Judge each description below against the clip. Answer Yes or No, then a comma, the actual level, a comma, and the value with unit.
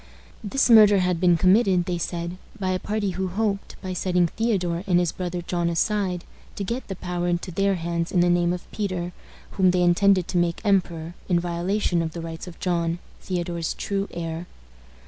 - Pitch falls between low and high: Yes, medium, 180 Hz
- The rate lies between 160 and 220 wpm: Yes, average, 190 wpm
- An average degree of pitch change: No, narrow, 2.1 semitones